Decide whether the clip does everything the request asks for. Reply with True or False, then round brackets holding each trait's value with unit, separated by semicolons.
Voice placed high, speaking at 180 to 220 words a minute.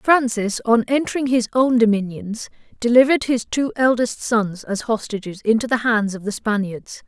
False (230 Hz; 160 wpm)